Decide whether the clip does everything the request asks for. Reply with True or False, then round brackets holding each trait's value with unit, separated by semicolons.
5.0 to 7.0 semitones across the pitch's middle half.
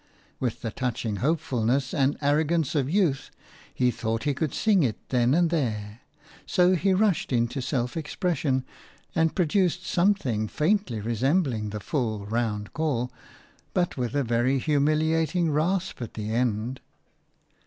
True (5.6 semitones)